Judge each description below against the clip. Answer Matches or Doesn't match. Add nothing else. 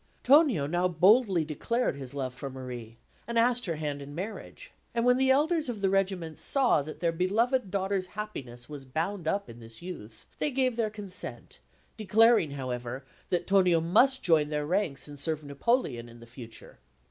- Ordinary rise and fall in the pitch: Doesn't match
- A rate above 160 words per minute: Matches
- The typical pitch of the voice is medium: Matches